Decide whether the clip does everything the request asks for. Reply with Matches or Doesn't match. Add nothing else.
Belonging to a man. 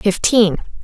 Doesn't match